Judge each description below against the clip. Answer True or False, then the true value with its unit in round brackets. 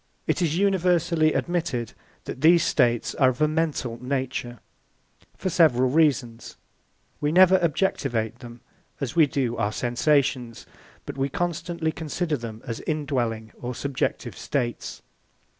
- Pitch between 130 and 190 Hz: True (140 Hz)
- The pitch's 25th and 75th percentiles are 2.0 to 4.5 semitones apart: False (5.2 semitones)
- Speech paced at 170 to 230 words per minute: False (135 wpm)